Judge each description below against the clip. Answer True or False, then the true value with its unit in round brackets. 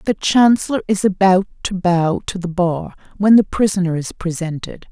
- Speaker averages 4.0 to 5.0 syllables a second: True (4.9 syllables/s)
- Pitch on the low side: False (185 Hz)